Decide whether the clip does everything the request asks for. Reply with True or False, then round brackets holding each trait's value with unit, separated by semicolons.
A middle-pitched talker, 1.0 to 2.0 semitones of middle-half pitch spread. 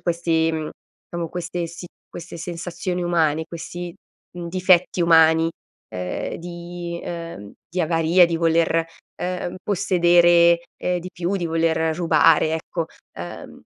True (170 Hz; 1.3 semitones)